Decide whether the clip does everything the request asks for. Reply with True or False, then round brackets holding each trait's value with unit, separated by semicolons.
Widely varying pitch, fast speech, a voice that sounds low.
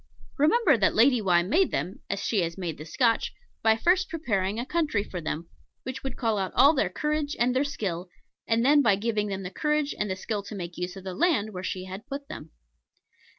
False (7.0 semitones; 225 wpm; 220 Hz)